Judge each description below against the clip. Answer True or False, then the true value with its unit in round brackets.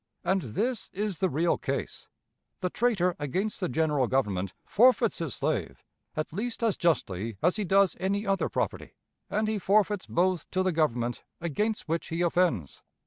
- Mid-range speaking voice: True (180 Hz)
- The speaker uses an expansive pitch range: False (5.0 semitones)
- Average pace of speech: True (165 wpm)